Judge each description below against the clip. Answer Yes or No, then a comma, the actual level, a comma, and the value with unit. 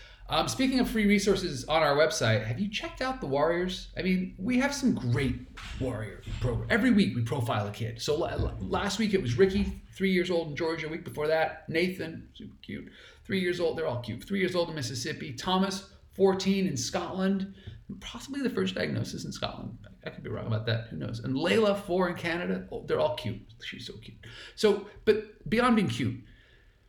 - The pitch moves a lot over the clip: Yes, wide, 8.0 semitones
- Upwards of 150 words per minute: Yes, fast, 205 wpm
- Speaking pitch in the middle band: Yes, medium, 175 Hz